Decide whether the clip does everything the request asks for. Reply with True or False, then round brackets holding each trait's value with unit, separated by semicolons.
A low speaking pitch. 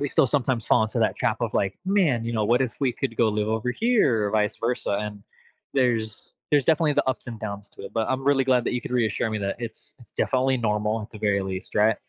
True (115 Hz)